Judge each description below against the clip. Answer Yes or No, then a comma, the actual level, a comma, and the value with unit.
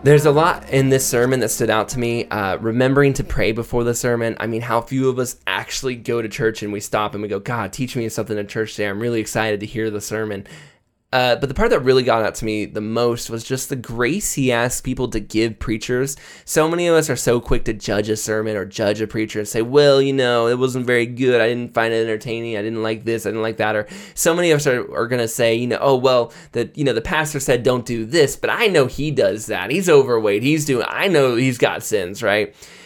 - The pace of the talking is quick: Yes, fast, 270 wpm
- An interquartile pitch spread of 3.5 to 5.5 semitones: No, average, 3.0 semitones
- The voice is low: Yes, low, 120 Hz